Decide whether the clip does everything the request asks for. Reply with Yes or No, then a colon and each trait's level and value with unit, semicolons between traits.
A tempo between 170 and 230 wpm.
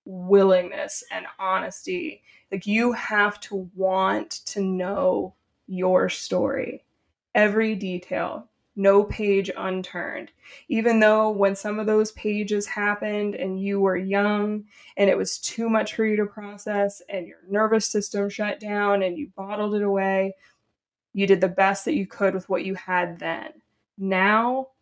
No: average, 150 wpm